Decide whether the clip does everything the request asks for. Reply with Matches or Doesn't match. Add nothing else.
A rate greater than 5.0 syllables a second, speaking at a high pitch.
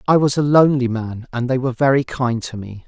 Doesn't match